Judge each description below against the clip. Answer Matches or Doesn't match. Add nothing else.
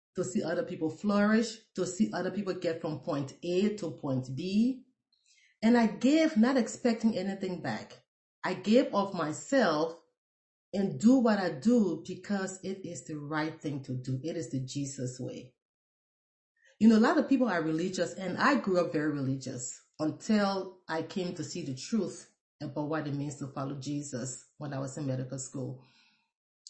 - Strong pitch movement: Matches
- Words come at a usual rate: Matches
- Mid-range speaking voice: Matches